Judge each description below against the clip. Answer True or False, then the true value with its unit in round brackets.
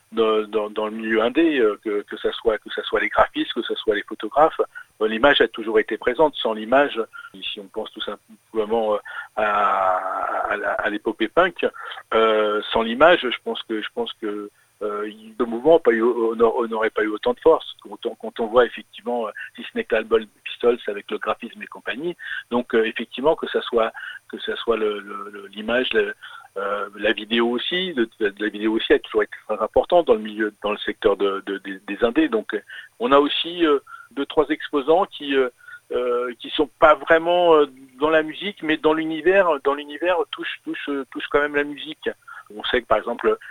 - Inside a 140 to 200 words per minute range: True (195 wpm)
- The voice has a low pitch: False (150 Hz)